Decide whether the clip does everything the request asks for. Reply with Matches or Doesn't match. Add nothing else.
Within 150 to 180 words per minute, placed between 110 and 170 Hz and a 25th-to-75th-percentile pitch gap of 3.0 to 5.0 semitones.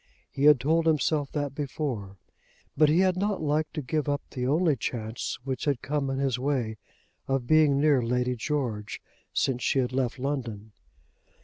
Matches